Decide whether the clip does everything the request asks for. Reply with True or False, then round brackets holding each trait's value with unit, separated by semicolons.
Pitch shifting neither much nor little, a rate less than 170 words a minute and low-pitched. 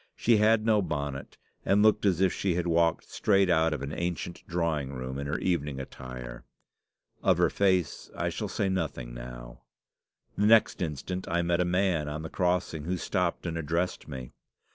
False (4.4 semitones; 185 wpm; 85 Hz)